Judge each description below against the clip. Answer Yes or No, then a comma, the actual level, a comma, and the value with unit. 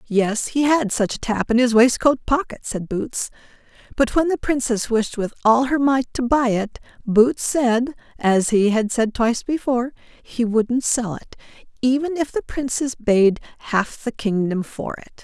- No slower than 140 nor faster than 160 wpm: No, average, 180 wpm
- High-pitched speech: Yes, high, 240 Hz